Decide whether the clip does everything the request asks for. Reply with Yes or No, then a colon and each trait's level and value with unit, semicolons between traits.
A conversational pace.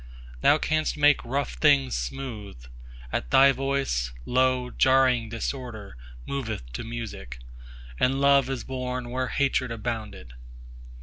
No: slow, 115 wpm